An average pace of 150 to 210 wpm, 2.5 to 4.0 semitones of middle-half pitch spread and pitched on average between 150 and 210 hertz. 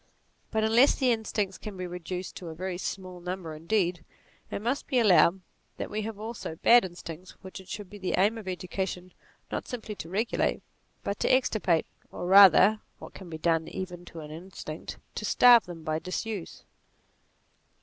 Yes: average, 180 wpm; average, 3.6 semitones; high, 190 Hz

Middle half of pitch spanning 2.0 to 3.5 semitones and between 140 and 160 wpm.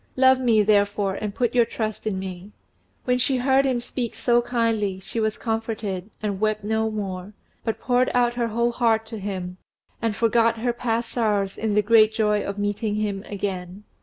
No: narrow, 2.6 semitones; average, 190 wpm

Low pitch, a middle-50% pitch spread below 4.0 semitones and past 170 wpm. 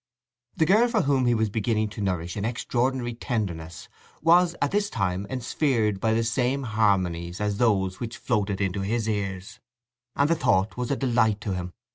No: low, 110 Hz; average, 4.4 semitones; average, 180 wpm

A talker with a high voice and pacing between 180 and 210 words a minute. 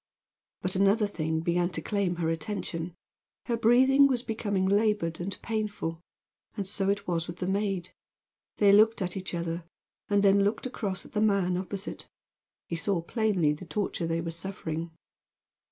No: high, 195 Hz; average, 165 wpm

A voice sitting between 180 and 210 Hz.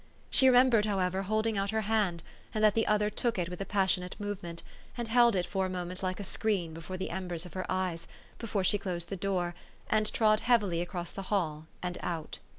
Yes: high, 190 Hz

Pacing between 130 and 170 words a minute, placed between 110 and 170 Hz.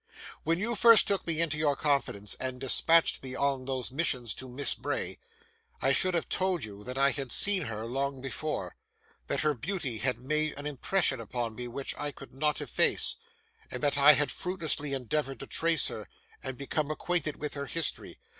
No: average, 190 wpm; medium, 140 Hz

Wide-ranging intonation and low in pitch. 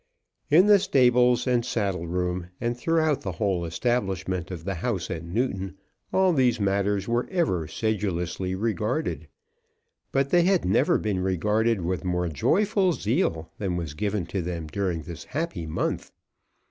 Yes: wide, 6.0 semitones; low, 100 Hz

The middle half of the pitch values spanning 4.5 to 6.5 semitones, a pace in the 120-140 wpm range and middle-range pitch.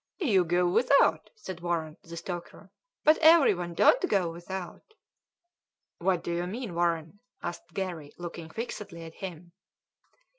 No: narrow, 2.6 semitones; slow, 135 wpm; medium, 175 Hz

